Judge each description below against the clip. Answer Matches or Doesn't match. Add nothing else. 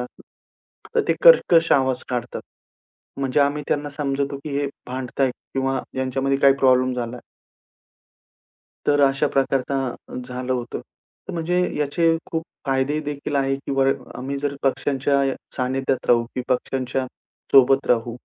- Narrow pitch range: Matches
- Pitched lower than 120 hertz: Doesn't match